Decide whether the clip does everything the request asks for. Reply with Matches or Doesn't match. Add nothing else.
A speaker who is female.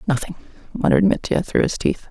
Matches